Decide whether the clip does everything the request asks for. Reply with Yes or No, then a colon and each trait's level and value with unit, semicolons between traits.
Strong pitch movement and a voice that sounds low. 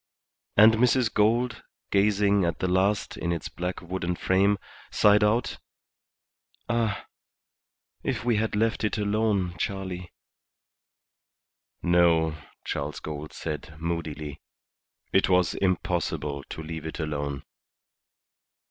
No: average, 4.4 semitones; very low, 90 Hz